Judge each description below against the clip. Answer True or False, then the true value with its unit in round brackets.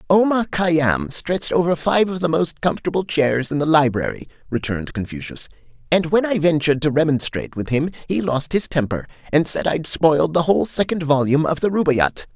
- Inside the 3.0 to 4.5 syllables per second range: False (5.6 syllables/s)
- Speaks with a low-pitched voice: False (155 Hz)